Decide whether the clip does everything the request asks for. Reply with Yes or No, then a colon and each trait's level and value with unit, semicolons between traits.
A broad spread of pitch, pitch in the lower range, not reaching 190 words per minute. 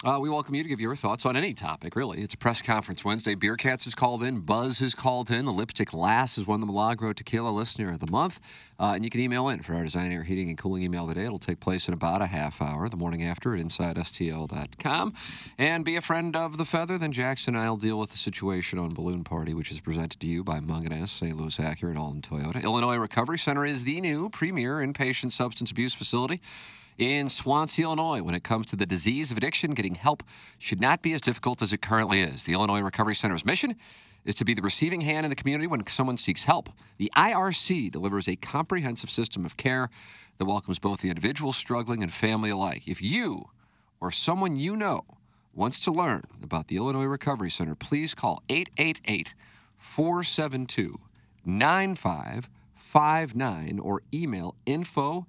No: wide, 6.5 semitones; low, 115 Hz; fast, 205 wpm